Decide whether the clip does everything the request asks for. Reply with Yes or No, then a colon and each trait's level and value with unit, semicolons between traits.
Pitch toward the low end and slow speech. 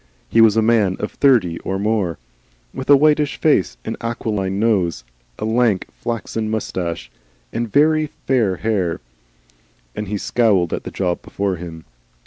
No: low, 110 Hz; average, 150 wpm